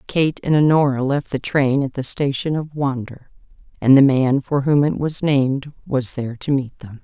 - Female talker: Yes, female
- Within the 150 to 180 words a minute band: No, fast, 205 wpm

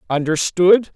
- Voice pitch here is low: No, medium, 180 Hz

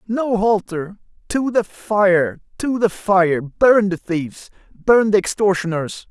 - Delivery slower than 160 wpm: Yes, average, 140 wpm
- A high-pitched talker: Yes, high, 195 Hz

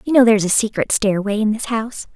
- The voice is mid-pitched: No, high, 220 Hz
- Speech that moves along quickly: Yes, fast, 250 wpm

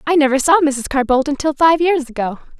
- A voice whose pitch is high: Yes, very high, 285 Hz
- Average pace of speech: No, fast, 230 wpm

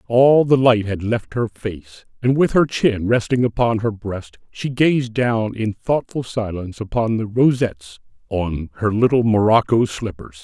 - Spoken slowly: No, average, 165 wpm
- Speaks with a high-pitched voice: No, low, 115 Hz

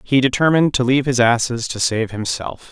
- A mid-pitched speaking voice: No, low, 125 Hz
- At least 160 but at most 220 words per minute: Yes, average, 200 wpm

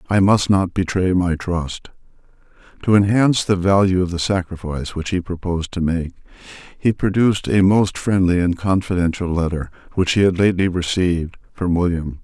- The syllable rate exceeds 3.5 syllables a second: Yes, 5.4 syllables/s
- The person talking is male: Yes, male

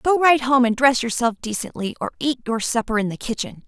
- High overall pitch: Yes, high, 245 Hz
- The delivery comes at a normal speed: No, fast, 210 wpm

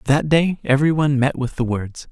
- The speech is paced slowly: No, average, 200 wpm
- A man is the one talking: Yes, male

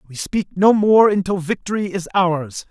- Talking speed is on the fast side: No, average, 180 wpm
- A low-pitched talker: No, medium, 185 Hz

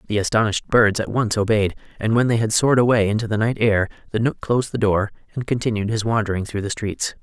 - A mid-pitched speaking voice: No, low, 110 Hz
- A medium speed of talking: No, fast, 235 wpm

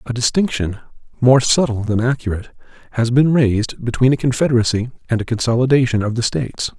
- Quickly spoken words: No, average, 160 wpm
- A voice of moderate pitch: No, low, 120 Hz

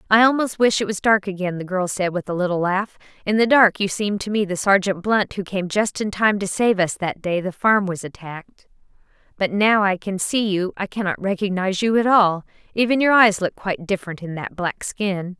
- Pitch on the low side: No, high, 195 Hz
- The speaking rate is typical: No, fast, 235 wpm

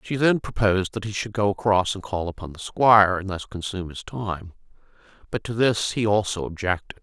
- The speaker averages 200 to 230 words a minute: Yes, fast, 205 wpm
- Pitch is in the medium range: No, low, 100 Hz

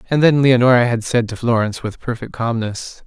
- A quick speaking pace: No, average, 195 wpm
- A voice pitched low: Yes, low, 120 Hz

